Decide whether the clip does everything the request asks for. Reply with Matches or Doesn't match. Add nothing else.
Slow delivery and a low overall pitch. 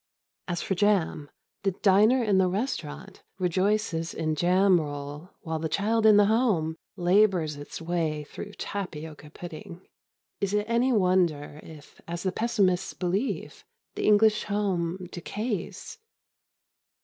Doesn't match